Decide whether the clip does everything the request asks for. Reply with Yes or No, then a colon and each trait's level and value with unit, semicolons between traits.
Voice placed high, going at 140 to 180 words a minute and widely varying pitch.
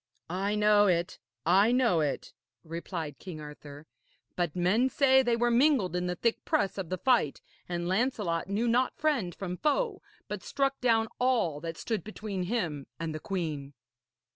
Yes: high, 195 Hz; average, 165 wpm; wide, 6.1 semitones